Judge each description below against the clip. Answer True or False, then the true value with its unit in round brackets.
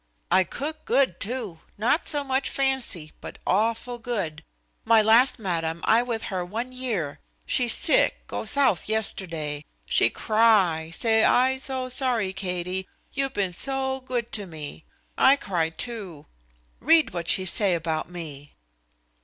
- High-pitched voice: True (220 Hz)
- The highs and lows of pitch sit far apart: True (6.6 semitones)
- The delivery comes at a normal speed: True (145 wpm)